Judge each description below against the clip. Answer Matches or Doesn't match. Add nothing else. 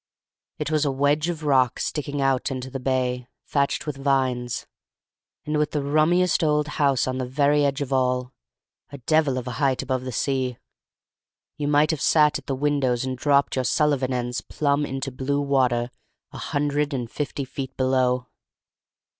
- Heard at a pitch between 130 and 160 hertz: Matches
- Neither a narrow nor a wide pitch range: Doesn't match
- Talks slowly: Doesn't match